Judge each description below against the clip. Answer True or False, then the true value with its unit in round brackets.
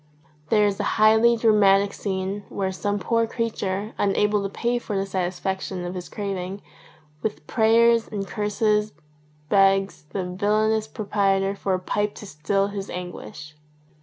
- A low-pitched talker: False (200 Hz)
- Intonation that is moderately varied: False (1.9 semitones)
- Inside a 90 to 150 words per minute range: True (145 wpm)